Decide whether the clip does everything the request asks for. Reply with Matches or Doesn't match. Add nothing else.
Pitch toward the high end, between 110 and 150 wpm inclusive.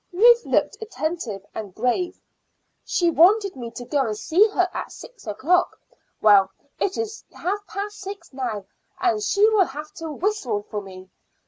Doesn't match